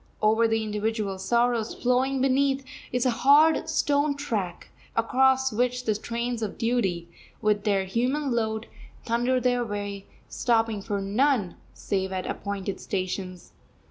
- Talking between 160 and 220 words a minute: No, slow, 135 wpm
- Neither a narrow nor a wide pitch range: Yes, average, 3.8 semitones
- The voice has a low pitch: No, high, 230 Hz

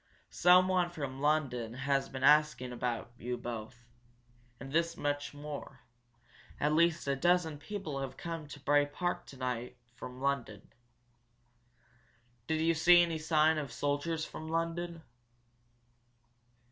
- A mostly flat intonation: No, average, 3.7 semitones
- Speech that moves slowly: Yes, slow, 130 wpm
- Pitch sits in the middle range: Yes, medium, 145 Hz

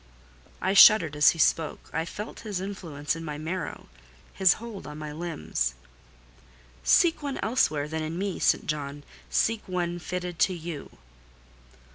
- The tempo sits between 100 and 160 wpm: Yes, average, 145 wpm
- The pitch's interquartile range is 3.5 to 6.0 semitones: Yes, average, 4.2 semitones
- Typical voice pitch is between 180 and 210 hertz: No, medium, 165 Hz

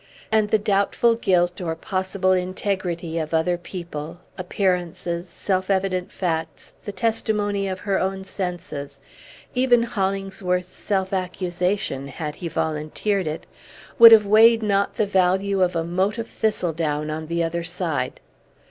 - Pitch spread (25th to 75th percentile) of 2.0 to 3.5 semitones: Yes, average, 2.8 semitones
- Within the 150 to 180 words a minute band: No, average, 140 wpm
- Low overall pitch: No, medium, 185 Hz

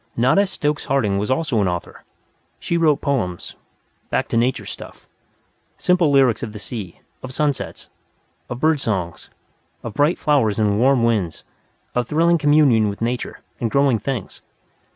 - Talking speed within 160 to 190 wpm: No, average, 150 wpm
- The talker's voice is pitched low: Yes, low, 125 Hz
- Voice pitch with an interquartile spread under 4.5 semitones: No, wide, 5.4 semitones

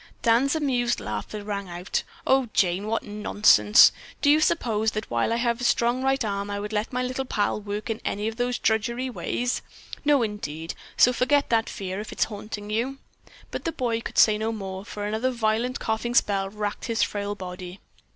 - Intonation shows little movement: No, average, 3.1 semitones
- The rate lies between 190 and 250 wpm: Yes, average, 195 wpm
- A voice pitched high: Yes, high, 220 Hz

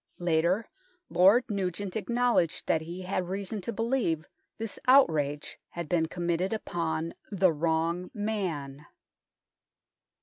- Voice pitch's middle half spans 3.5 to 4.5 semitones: Yes, average, 4.1 semitones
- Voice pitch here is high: No, medium, 180 Hz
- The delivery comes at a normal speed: No, slow, 110 wpm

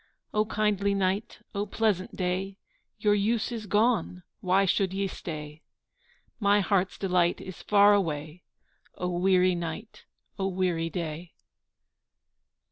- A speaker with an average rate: No, slow, 125 wpm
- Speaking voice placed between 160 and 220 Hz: Yes, high, 190 Hz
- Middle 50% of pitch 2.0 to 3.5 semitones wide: Yes, narrow, 2.4 semitones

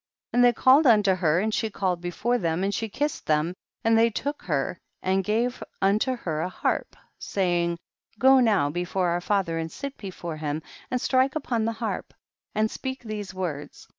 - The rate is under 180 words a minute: No, average, 195 wpm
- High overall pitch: Yes, high, 200 Hz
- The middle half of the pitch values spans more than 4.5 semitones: Yes, wide, 5.4 semitones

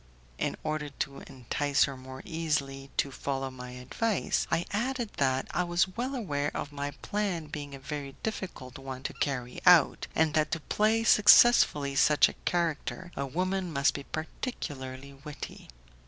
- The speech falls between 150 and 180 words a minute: Yes, average, 160 wpm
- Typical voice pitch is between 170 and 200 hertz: No, medium, 145 Hz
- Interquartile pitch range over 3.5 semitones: Yes, average, 4.7 semitones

